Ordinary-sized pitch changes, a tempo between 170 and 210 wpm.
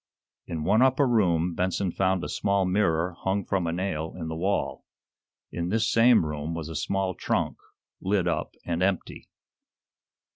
No: average, 3.2 semitones; average, 160 wpm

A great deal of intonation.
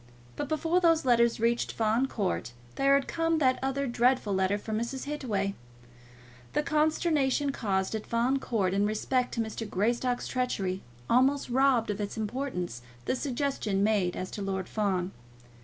No: average, 5.0 semitones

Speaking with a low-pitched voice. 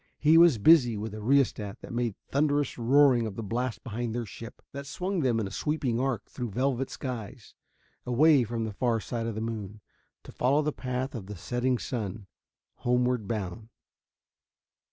Yes: low, 120 Hz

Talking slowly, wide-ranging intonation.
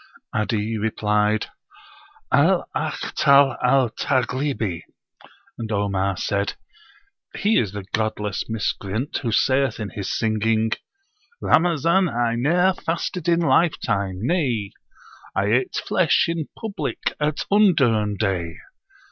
Yes: slow, 105 wpm; wide, 6.3 semitones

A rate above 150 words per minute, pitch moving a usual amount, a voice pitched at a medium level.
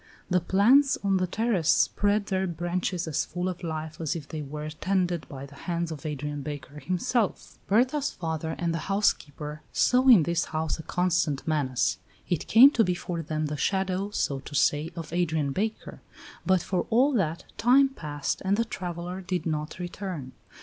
Yes: average, 180 wpm; average, 4.1 semitones; medium, 175 Hz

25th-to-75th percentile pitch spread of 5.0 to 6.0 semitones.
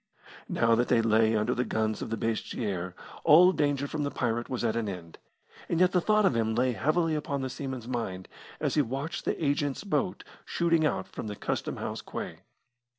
Yes: average, 5.3 semitones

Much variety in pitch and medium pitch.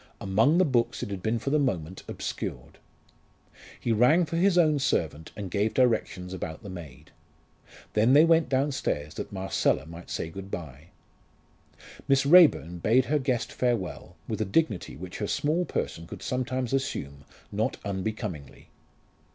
No: wide, 7.1 semitones; low, 110 Hz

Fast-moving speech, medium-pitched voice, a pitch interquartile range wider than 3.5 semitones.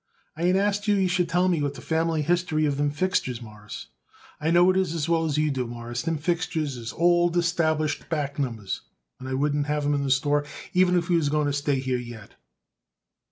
Yes: fast, 215 wpm; medium, 150 Hz; average, 3.9 semitones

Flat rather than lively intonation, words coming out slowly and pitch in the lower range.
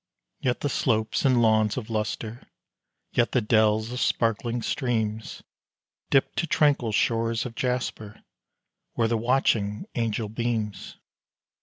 Yes: narrow, 2.2 semitones; slow, 125 wpm; low, 115 Hz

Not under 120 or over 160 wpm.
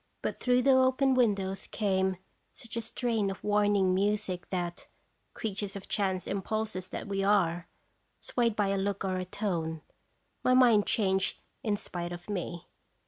Yes: average, 155 wpm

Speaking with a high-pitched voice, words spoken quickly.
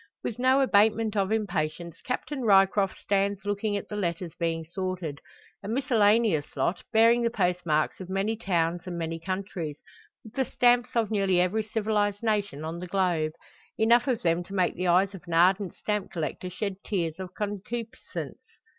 No: high, 195 Hz; average, 170 wpm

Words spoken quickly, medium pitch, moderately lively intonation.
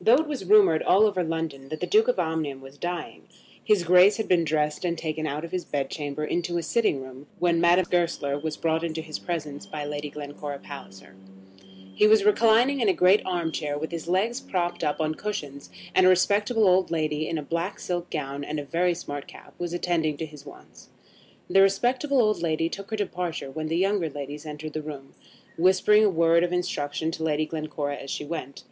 Yes: fast, 215 wpm; medium, 165 Hz; average, 3.7 semitones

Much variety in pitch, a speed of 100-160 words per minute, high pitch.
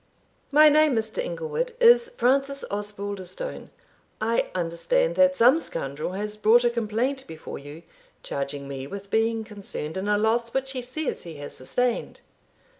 Yes: wide, 6.5 semitones; average, 150 wpm; high, 225 Hz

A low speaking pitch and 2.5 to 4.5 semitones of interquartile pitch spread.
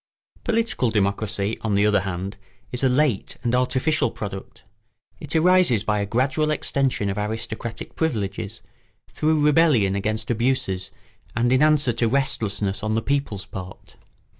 No: low, 115 Hz; wide, 5.4 semitones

